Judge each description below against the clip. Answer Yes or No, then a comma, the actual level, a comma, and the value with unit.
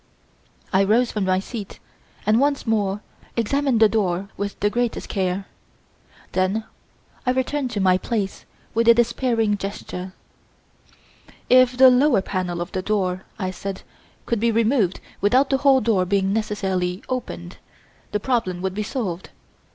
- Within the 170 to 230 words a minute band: No, average, 150 wpm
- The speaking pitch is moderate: No, high, 210 Hz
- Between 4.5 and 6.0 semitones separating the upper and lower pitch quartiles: No, average, 4.1 semitones